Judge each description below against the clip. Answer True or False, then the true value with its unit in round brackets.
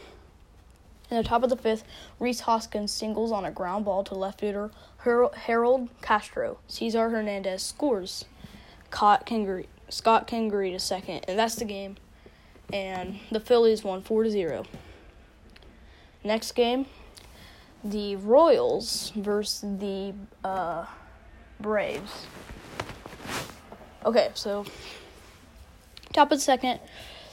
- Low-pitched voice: False (215 Hz)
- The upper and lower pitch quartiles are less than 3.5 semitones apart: True (2.8 semitones)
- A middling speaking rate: False (110 wpm)